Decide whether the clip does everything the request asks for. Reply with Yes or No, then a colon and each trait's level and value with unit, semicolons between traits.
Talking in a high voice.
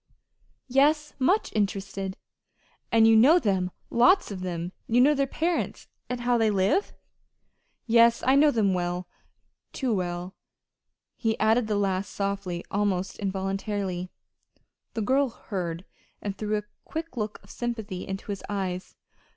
Yes: high, 210 Hz